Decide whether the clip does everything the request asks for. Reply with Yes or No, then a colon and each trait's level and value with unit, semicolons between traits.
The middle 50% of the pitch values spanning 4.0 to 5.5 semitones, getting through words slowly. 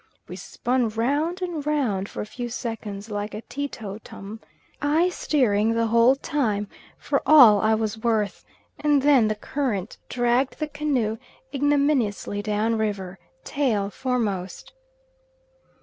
Yes: average, 5.1 semitones; slow, 130 wpm